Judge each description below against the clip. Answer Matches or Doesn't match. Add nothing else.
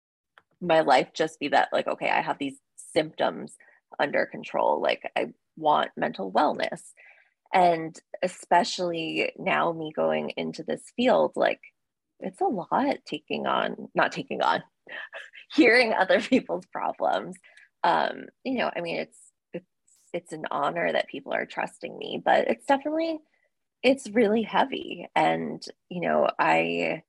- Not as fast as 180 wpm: Matches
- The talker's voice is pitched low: Doesn't match